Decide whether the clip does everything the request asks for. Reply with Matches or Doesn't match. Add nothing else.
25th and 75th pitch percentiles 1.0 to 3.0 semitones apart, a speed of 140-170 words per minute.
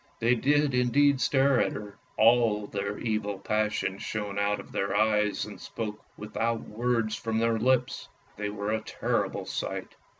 Matches